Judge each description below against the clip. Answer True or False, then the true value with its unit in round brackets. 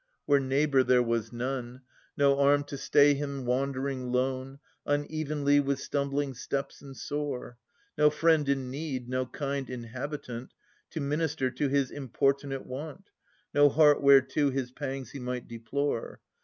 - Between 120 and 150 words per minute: True (140 wpm)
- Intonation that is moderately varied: False (2.0 semitones)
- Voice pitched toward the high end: False (140 Hz)